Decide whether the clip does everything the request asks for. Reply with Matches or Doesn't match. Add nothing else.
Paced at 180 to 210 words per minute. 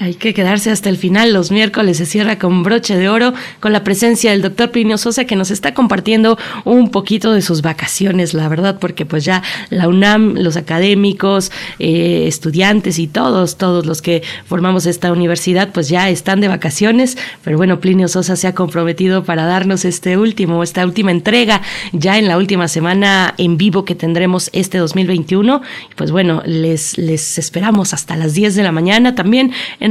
Matches